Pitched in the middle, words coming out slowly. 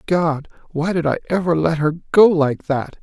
No: medium, 160 Hz; average, 180 wpm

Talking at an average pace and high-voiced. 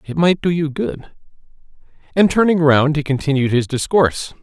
No: average, 165 wpm; medium, 150 Hz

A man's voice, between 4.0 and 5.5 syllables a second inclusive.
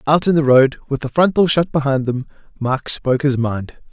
Yes: male; 5.3 syllables/s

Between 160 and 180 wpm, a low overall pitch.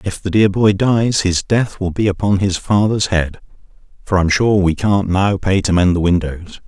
No: fast, 205 wpm; very low, 95 Hz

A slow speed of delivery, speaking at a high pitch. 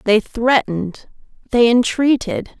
Yes: slow, 90 wpm; high, 235 Hz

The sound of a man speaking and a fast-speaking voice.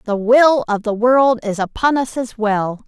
No: female; fast, 210 wpm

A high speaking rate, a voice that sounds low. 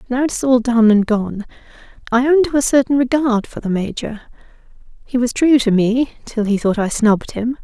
No: fast, 210 wpm; high, 240 Hz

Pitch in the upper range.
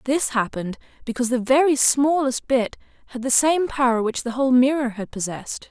Yes: very high, 255 Hz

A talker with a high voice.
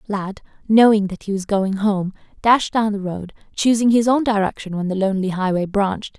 Yes: high, 205 Hz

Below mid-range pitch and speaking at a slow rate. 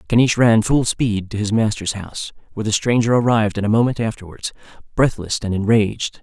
No: low, 110 Hz; average, 175 wpm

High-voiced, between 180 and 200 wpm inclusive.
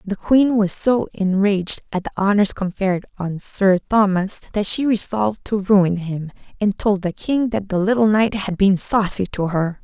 Yes: high, 200 Hz; average, 190 wpm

